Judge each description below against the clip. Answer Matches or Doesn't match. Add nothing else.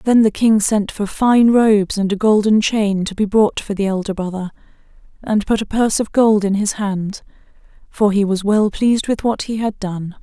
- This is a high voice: Matches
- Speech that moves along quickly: Matches